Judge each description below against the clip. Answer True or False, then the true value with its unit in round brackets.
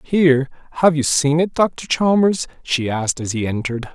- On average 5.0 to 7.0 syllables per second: True (5.3 syllables/s)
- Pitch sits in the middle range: True (150 Hz)